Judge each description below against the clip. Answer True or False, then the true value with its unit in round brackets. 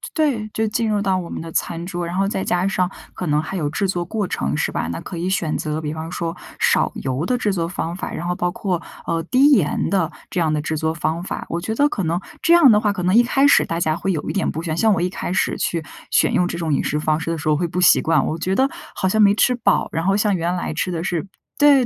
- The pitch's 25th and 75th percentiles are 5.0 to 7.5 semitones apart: False (3.7 semitones)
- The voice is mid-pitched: True (175 Hz)